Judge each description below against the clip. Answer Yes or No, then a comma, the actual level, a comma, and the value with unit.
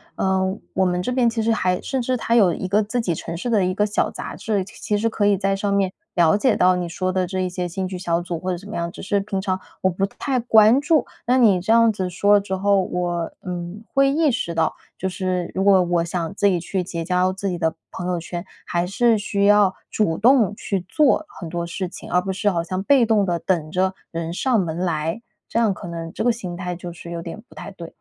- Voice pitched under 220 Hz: Yes, high, 190 Hz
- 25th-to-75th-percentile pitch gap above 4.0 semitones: No, average, 3.1 semitones